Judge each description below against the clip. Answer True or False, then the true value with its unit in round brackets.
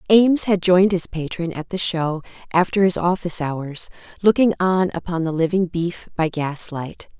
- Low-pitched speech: False (175 Hz)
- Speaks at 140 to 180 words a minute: True (165 wpm)